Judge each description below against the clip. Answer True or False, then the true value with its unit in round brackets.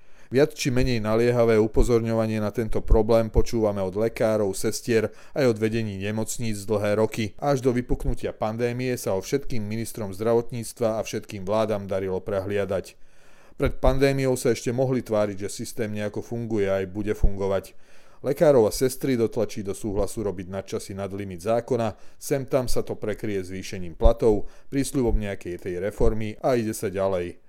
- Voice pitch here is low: True (110 Hz)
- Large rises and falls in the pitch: False (2.9 semitones)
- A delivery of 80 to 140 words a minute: False (155 wpm)